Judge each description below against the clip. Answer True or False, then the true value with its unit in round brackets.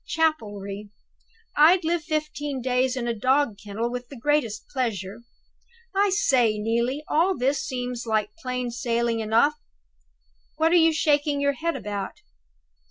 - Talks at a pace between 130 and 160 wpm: True (140 wpm)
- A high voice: True (255 Hz)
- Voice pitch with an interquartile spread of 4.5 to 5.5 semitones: True (4.9 semitones)